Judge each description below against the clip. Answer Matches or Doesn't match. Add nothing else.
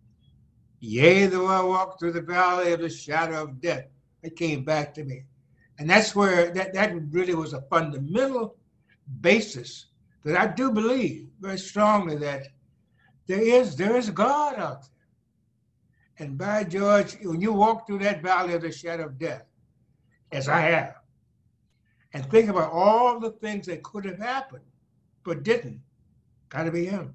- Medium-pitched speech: Matches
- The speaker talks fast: Doesn't match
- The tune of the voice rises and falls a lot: Matches